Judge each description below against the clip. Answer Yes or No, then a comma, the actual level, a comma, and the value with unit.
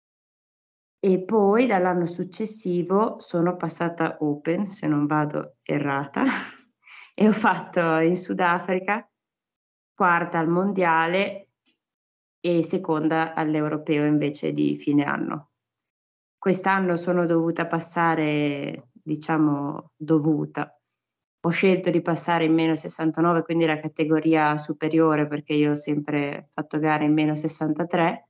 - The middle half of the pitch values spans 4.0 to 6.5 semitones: No, average, 2.7 semitones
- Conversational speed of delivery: No, slow, 110 wpm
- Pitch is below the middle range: No, medium, 165 Hz